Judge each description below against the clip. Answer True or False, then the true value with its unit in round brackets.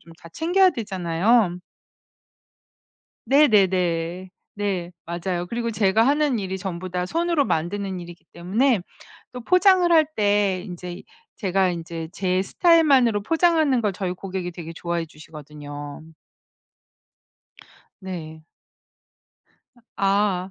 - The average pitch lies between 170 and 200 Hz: True (190 Hz)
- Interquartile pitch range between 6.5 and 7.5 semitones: False (5.1 semitones)